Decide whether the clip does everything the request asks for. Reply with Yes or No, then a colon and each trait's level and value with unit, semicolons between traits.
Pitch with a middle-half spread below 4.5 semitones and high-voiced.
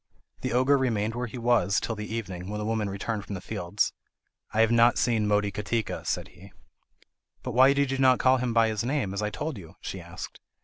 No: average, 3.3 semitones; low, 110 Hz